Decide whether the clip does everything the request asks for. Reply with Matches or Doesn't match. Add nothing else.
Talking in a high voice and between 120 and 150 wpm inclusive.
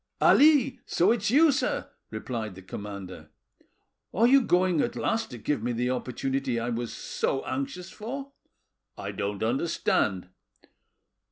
Doesn't match